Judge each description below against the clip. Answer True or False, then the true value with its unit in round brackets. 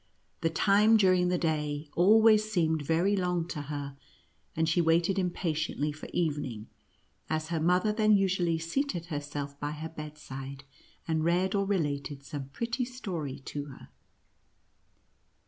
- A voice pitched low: False (165 Hz)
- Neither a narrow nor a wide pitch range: True (4.3 semitones)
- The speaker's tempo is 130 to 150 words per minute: True (140 wpm)